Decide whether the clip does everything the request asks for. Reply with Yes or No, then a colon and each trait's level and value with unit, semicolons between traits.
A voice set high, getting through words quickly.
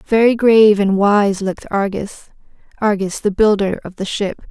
No: high, 205 Hz; average, 145 wpm